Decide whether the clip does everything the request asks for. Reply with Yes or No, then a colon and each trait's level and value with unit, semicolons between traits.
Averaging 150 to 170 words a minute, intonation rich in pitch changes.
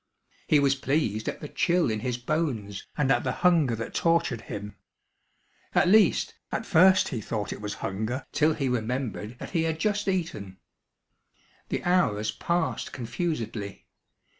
Yes: average, 155 wpm; wide, 7.2 semitones